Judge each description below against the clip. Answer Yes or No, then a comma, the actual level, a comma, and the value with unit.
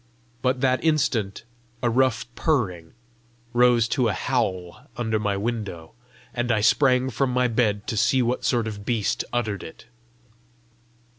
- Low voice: Yes, low, 120 Hz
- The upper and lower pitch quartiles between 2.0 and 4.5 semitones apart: Yes, average, 3.5 semitones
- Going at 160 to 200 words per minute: No, average, 145 wpm